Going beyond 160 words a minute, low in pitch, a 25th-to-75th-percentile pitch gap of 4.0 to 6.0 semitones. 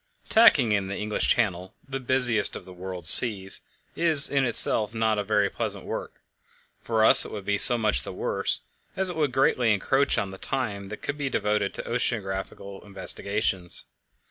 Yes: average, 180 wpm; low, 105 Hz; average, 4.5 semitones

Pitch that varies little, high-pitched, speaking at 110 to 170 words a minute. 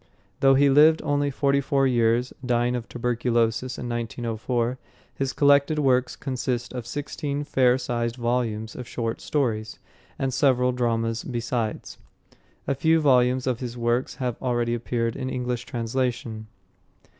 No: narrow, 2.2 semitones; low, 125 Hz; average, 140 wpm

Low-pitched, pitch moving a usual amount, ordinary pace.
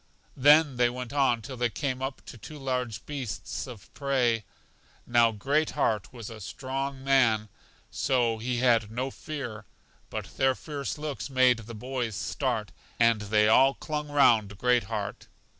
Yes: low, 125 Hz; average, 3.3 semitones; average, 160 wpm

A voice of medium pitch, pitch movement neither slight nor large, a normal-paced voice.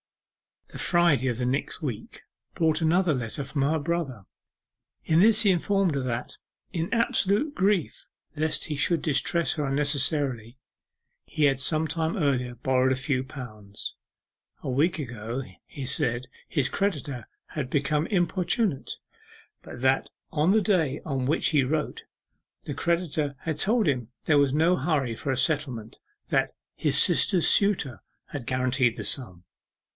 Yes: medium, 145 Hz; average, 4.5 semitones; average, 150 wpm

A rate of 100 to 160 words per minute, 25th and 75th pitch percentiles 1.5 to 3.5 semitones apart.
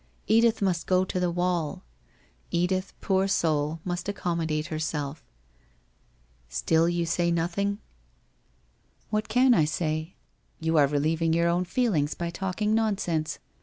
Yes: average, 140 wpm; average, 3.1 semitones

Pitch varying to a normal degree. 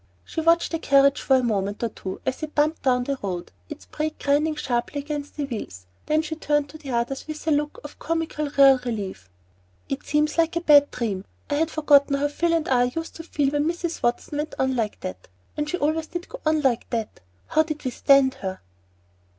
Yes: average, 3.8 semitones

